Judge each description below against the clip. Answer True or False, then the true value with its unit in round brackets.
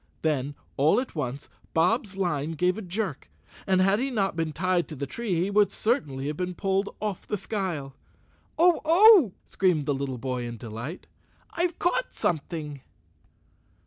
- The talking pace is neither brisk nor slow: True (165 wpm)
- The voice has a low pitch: False (180 Hz)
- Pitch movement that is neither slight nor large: False (6.4 semitones)